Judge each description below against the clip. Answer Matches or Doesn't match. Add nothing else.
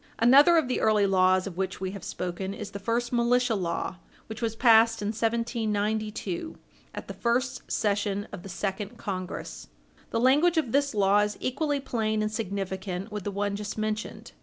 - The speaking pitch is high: Matches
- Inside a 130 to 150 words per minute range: Doesn't match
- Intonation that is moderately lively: Matches